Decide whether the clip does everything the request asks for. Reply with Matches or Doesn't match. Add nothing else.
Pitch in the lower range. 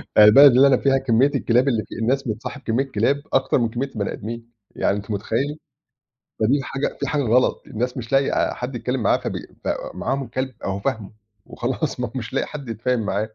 Matches